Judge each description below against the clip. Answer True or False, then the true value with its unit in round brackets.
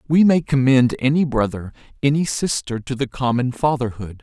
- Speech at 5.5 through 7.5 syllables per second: False (5.1 syllables/s)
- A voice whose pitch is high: False (130 Hz)